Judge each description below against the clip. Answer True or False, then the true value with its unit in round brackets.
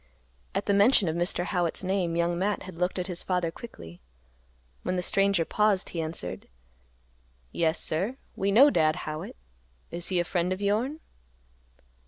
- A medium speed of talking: True (160 wpm)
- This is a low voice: False (180 Hz)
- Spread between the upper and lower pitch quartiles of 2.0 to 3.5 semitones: True (2.9 semitones)